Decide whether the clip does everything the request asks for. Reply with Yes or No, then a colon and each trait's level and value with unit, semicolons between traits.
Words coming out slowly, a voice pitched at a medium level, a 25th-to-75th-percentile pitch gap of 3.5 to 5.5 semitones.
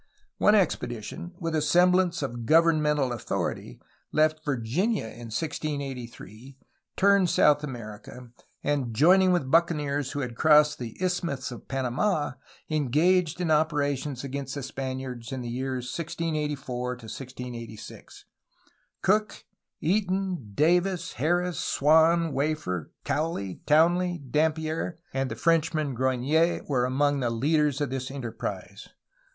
Yes: slow, 120 wpm; medium, 145 Hz; average, 4.5 semitones